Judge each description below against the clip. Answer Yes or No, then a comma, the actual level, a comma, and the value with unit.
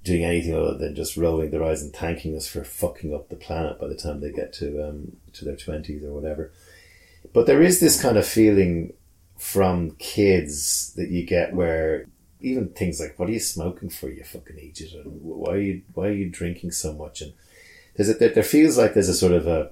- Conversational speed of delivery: No, fast, 220 wpm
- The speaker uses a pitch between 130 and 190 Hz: No, very low, 85 Hz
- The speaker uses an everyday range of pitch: Yes, average, 3.1 semitones